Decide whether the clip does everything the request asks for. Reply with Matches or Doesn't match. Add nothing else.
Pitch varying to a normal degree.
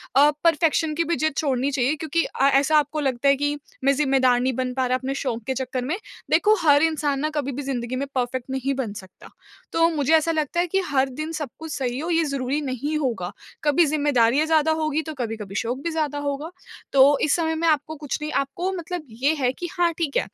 Matches